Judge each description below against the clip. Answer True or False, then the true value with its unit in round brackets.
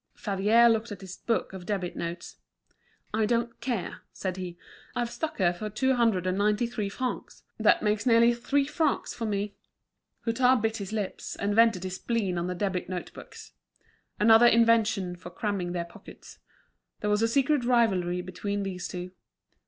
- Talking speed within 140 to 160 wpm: False (170 wpm)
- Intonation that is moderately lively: True (4.0 semitones)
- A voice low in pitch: False (210 Hz)